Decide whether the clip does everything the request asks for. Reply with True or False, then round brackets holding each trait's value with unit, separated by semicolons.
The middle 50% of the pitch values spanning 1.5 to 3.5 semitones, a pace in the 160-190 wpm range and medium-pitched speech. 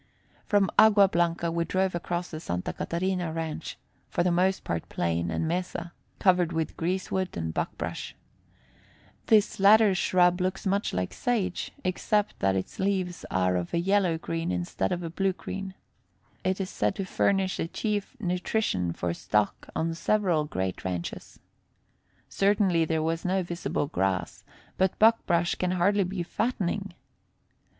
False (3.1 semitones; 150 wpm; 175 Hz)